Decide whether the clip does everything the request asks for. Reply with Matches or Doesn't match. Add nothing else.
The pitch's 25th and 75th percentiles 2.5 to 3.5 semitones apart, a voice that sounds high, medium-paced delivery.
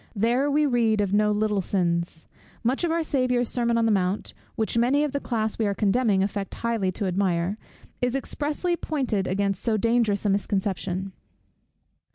Doesn't match